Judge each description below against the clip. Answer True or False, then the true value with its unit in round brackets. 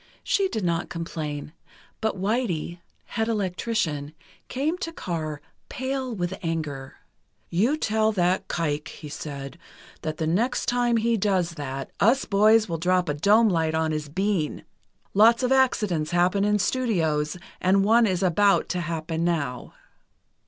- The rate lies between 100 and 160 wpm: True (145 wpm)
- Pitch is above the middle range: False (180 Hz)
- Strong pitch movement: True (5.7 semitones)